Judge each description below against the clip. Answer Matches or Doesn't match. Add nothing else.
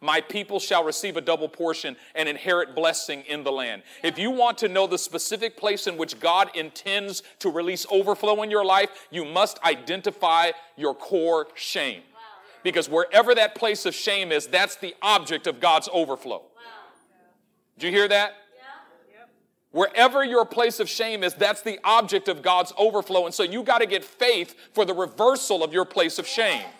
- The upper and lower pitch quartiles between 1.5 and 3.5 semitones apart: Doesn't match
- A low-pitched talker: Doesn't match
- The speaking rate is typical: Matches